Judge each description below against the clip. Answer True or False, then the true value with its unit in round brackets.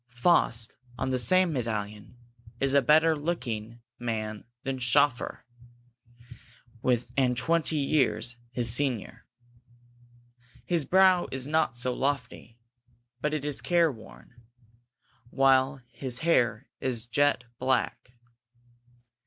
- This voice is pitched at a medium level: False (130 Hz)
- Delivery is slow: True (105 wpm)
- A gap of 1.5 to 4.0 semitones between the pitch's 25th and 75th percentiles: True (3.7 semitones)